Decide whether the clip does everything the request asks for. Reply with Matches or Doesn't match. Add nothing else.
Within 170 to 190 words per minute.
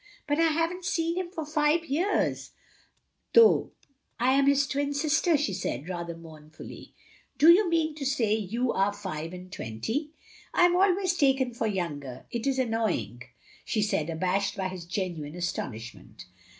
Matches